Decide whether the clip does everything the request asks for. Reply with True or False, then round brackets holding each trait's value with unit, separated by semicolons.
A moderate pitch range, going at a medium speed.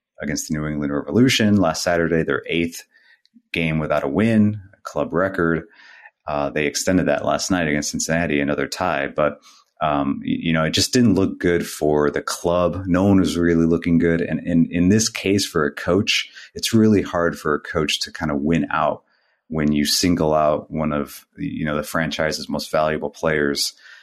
True (3.4 semitones; 190 wpm)